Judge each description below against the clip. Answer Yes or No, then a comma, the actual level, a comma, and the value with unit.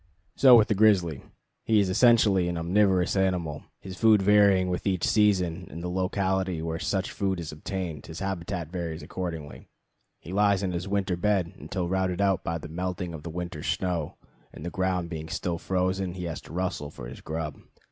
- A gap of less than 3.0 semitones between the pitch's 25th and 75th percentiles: Yes, narrow, 2.5 semitones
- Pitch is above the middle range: No, very low, 90 Hz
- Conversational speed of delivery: Yes, average, 190 wpm